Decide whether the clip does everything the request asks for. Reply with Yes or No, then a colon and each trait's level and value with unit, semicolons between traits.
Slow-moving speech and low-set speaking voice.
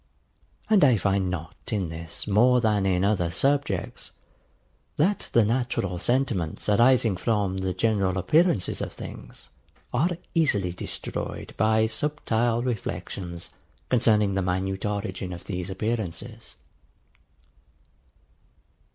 Yes: slow, 110 wpm; low, 105 Hz